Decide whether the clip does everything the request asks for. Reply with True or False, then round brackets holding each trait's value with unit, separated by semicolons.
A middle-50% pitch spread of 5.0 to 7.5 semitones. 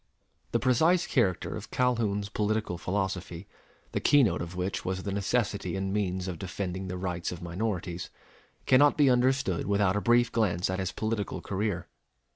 False (3.8 semitones)